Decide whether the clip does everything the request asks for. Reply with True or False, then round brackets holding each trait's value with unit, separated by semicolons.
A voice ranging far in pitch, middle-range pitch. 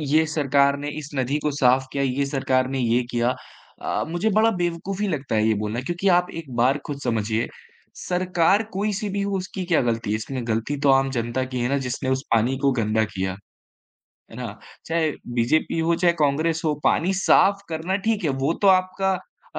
True (5.8 semitones; 145 Hz)